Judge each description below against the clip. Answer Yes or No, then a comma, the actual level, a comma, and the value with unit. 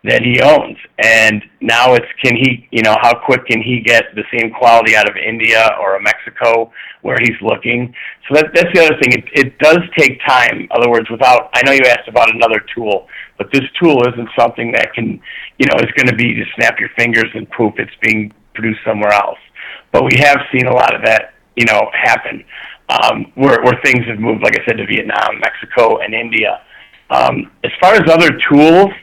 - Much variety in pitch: No, average, 3.5 semitones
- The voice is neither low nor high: No, low, 120 Hz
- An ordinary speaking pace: No, fast, 215 wpm